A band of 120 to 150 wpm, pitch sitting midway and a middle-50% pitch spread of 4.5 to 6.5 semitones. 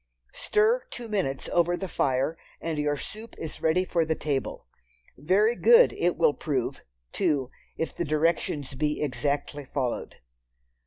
Yes: average, 145 wpm; medium, 155 Hz; average, 4.8 semitones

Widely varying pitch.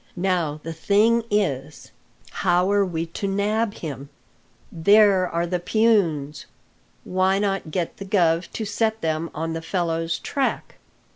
No: average, 3.8 semitones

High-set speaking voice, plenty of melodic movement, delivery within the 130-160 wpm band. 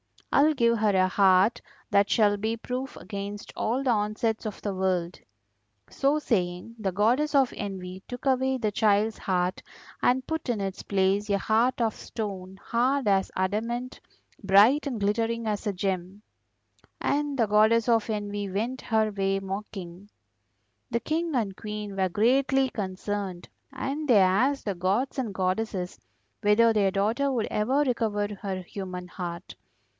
No: high, 210 Hz; average, 3.7 semitones; average, 155 wpm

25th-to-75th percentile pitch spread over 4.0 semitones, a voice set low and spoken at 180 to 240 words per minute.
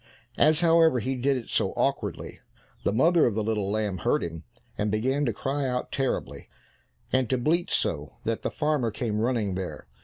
Yes: average, 4.9 semitones; low, 120 Hz; average, 185 wpm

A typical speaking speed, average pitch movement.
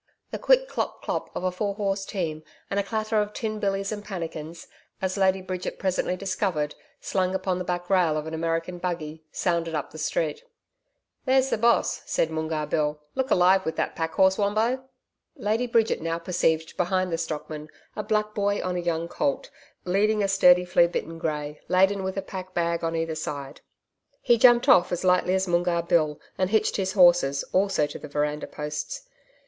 Yes: average, 185 wpm; average, 3.5 semitones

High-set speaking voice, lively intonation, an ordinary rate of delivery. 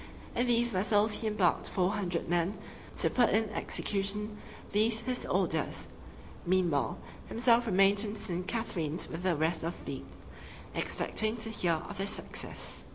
No: high, 205 Hz; average, 3.8 semitones; average, 155 wpm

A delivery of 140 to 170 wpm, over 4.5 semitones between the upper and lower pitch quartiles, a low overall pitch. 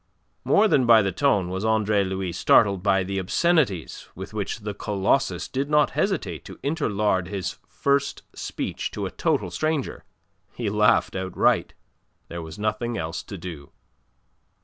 Yes: average, 150 wpm; wide, 5.6 semitones; low, 105 Hz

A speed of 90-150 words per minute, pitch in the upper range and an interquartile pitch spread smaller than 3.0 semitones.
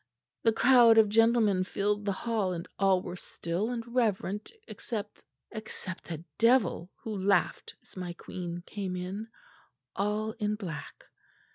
No: average, 140 wpm; high, 205 Hz; average, 3.3 semitones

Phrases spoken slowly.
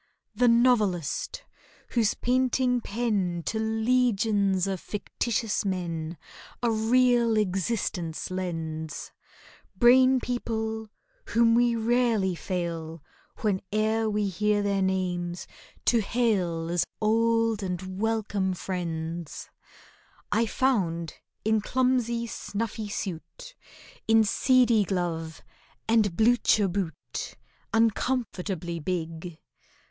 Yes: slow, 90 wpm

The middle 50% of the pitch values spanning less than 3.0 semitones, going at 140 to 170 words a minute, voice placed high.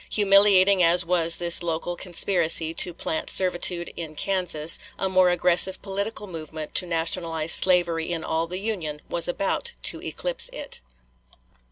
No: narrow, 2.6 semitones; average, 145 wpm; medium, 175 Hz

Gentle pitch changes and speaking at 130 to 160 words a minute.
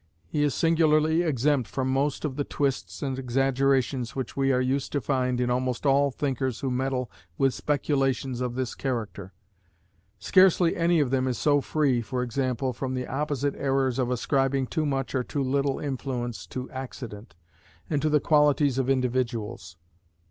No: narrow, 2.1 semitones; average, 170 wpm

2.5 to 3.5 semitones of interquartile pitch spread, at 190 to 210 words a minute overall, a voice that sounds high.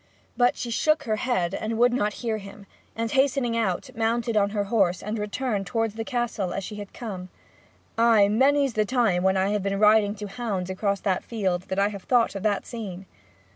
Yes: average, 2.9 semitones; fast, 205 wpm; high, 210 Hz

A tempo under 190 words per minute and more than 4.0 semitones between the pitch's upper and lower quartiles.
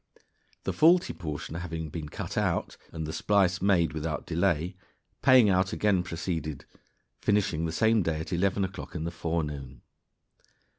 No: average, 150 wpm; average, 3.5 semitones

